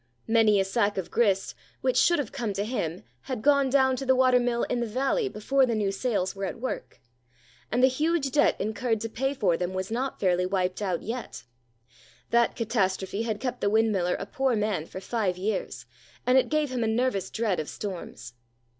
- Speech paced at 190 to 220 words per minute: Yes, average, 200 wpm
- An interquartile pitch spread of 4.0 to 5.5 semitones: Yes, average, 4.7 semitones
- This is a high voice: Yes, high, 225 Hz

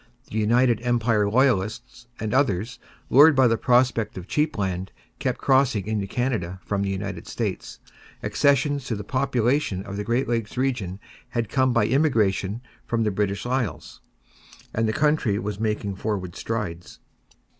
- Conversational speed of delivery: Yes, average, 155 wpm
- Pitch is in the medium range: No, low, 115 Hz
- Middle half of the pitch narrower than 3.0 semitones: No, average, 4.1 semitones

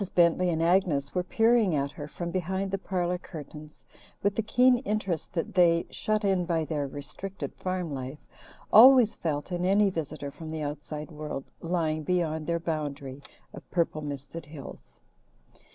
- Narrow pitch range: No, average, 3.8 semitones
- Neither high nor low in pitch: Yes, medium, 170 Hz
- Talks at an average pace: Yes, average, 160 wpm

